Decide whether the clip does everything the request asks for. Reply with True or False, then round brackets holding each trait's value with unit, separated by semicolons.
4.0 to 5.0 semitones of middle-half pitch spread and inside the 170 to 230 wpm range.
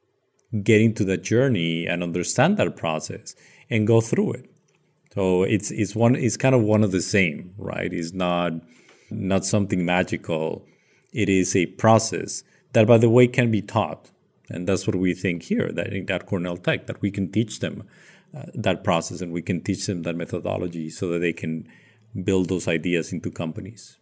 True (4.4 semitones; 185 wpm)